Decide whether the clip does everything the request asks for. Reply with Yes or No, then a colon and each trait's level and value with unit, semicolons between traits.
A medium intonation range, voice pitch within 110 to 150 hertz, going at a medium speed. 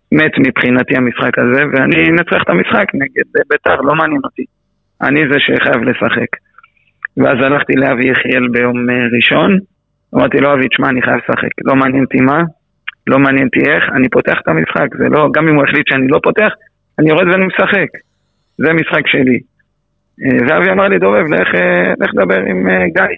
No: average, 4.7 semitones; low, 135 Hz; fast, 175 wpm